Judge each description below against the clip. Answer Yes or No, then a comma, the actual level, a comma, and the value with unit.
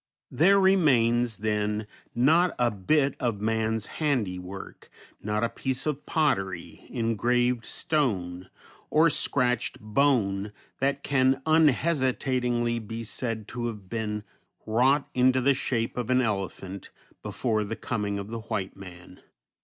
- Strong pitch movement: No, average, 4.0 semitones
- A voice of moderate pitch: No, low, 120 Hz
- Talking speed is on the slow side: Yes, slow, 125 wpm